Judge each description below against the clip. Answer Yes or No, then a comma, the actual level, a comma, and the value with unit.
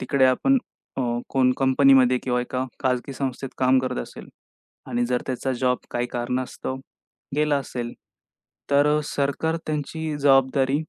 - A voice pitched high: No, low, 130 Hz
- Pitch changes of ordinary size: No, narrow, 1.8 semitones